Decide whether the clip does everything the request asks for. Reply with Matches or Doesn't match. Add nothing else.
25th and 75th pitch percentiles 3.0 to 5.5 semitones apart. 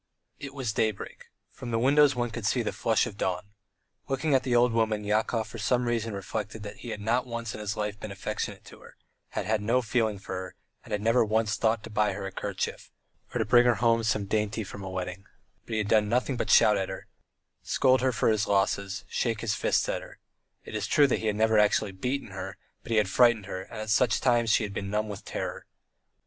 Doesn't match